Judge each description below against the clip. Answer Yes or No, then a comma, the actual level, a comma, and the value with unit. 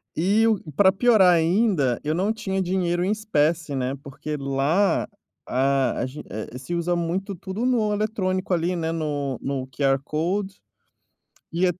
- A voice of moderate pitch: Yes, medium, 175 Hz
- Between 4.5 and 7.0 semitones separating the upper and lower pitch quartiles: Yes, average, 5.3 semitones